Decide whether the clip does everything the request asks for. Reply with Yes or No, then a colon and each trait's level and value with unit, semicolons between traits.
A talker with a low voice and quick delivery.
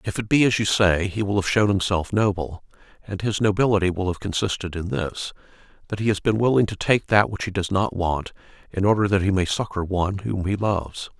Yes: low, 100 Hz; fast, 230 wpm